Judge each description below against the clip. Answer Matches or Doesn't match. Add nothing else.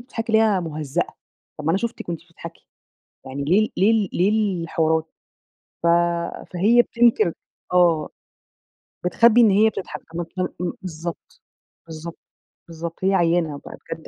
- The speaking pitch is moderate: Matches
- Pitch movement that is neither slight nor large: Matches